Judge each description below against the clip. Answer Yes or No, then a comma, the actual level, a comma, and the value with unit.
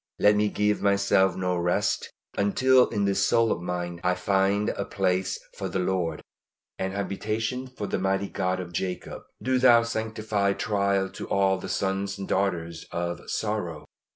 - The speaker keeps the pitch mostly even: Yes, narrow, 2.2 semitones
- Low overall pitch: Yes, low, 100 Hz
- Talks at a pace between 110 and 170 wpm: Yes, average, 165 wpm